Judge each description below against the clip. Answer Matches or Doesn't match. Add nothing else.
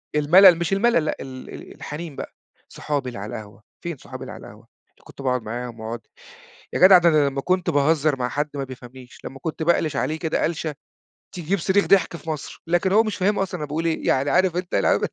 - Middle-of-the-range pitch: Matches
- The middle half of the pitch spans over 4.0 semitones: Matches